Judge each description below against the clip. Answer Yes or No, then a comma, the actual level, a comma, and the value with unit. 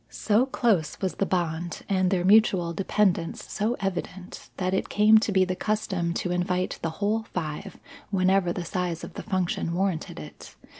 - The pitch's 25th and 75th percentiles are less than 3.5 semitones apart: Yes, narrow, 2.6 semitones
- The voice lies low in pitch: No, medium, 185 Hz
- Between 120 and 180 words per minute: Yes, average, 170 wpm